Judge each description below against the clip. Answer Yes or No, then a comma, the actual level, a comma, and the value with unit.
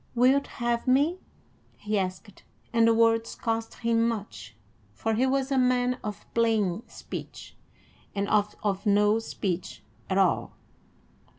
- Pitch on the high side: Yes, high, 225 Hz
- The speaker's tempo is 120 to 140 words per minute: Yes, slow, 135 wpm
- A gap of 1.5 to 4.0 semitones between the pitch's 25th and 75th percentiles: Yes, average, 3.1 semitones